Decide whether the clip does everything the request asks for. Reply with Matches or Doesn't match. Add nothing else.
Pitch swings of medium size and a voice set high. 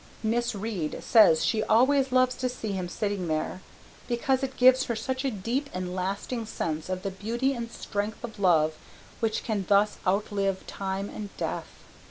Matches